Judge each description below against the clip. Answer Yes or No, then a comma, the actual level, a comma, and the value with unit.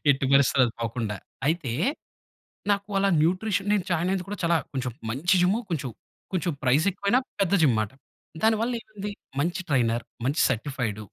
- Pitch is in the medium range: Yes, medium, 160 Hz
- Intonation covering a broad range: Yes, wide, 7.3 semitones